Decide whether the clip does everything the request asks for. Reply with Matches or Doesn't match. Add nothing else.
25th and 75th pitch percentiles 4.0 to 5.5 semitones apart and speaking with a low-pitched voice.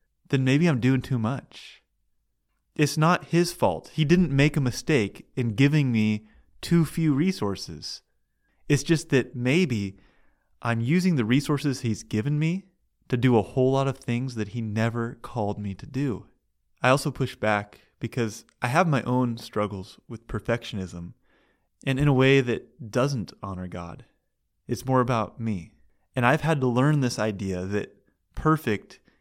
Matches